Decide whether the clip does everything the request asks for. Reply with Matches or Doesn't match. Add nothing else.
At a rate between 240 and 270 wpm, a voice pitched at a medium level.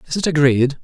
Doesn't match